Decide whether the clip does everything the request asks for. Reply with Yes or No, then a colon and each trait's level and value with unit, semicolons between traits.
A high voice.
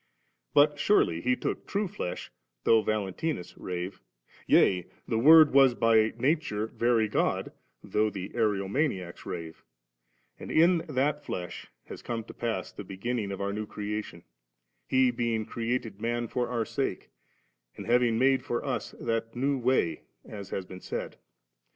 No: low, 115 Hz